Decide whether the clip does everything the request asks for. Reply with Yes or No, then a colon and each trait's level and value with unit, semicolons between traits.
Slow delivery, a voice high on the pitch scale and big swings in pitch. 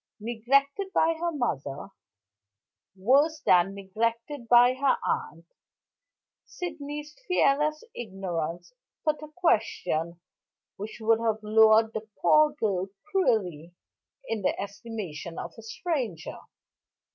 Yes: slow, 105 wpm; high, 225 Hz; wide, 7.1 semitones